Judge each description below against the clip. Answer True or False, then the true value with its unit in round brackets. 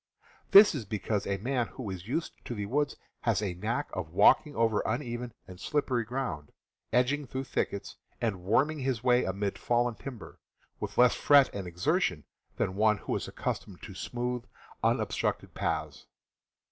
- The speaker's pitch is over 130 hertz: False (120 Hz)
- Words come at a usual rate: True (160 wpm)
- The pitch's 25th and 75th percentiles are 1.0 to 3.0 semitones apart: False (4.7 semitones)